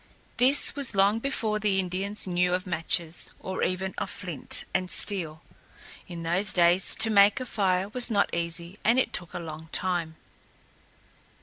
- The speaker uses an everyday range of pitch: Yes, average, 3.2 semitones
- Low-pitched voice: No, medium, 185 Hz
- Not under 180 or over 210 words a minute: No, average, 165 wpm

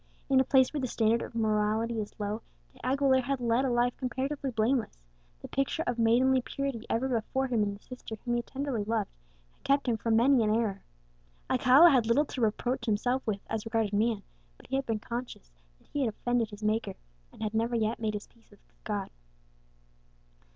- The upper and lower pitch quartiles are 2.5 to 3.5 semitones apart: Yes, average, 3.1 semitones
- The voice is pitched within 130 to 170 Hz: No, high, 235 Hz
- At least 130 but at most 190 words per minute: No, fast, 205 wpm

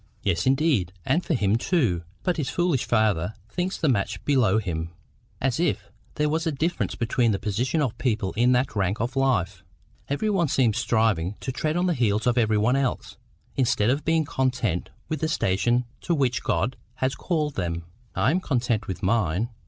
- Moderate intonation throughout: No, wide, 6.1 semitones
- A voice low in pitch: Yes, low, 125 Hz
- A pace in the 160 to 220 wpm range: Yes, average, 190 wpm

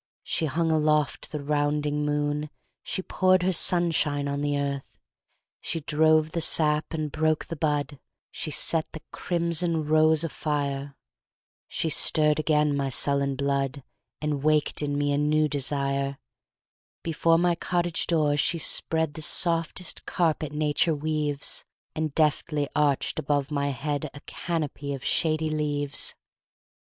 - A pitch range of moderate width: No, narrow, 1.7 semitones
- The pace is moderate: No, slow, 120 wpm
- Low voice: No, medium, 150 Hz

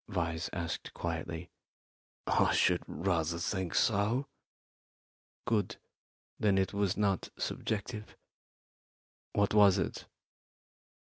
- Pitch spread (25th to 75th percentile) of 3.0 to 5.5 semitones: Yes, average, 3.5 semitones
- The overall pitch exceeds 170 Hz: No, very low, 95 Hz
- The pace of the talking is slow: Yes, slow, 90 wpm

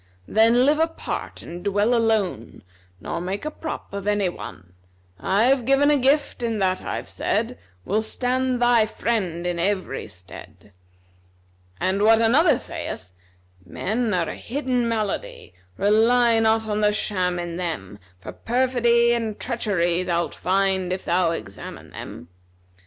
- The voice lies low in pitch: No, high, 210 Hz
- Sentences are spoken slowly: No, average, 145 wpm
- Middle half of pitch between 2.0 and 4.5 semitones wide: No, average, 4.9 semitones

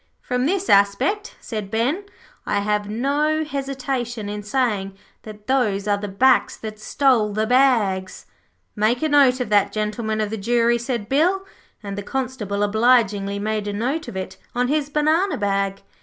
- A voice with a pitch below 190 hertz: No, high, 225 Hz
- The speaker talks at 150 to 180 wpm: Yes, average, 165 wpm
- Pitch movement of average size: Yes, average, 4.6 semitones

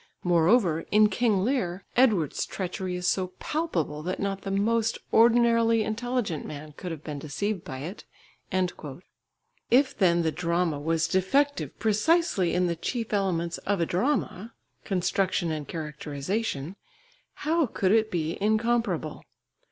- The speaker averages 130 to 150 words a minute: Yes, slow, 135 wpm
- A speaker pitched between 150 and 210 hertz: Yes, high, 190 Hz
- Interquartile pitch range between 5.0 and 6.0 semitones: Yes, average, 5.3 semitones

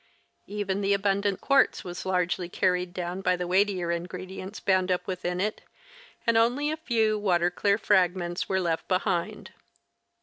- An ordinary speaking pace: Yes, average, 160 wpm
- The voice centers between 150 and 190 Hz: Yes, medium, 185 Hz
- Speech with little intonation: Yes, narrow, 2.2 semitones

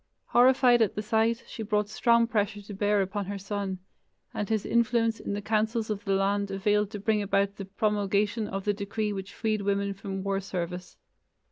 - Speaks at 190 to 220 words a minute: Yes, average, 195 wpm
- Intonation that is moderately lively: No, narrow, 1.8 semitones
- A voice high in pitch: Yes, high, 205 Hz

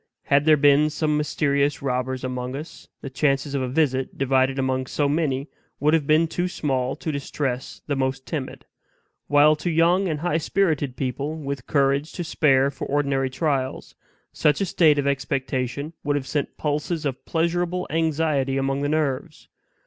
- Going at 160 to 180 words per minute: Yes, average, 170 wpm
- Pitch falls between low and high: Yes, medium, 145 Hz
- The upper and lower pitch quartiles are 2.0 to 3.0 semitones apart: Yes, narrow, 2.6 semitones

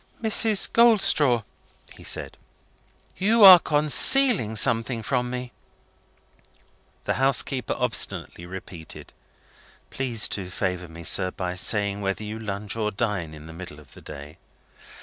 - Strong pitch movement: Yes, wide, 6.5 semitones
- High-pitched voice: No, low, 110 Hz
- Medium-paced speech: No, slow, 130 wpm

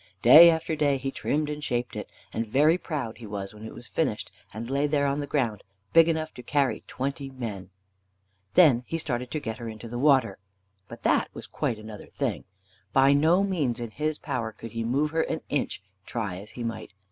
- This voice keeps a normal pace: No, fast, 210 wpm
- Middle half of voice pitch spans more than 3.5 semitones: Yes, average, 4.8 semitones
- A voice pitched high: No, low, 130 Hz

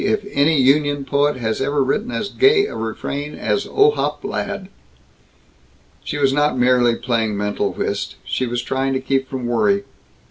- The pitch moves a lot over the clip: No, average, 3.4 semitones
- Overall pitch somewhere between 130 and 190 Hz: Yes, low, 135 Hz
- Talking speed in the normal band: Yes, average, 165 wpm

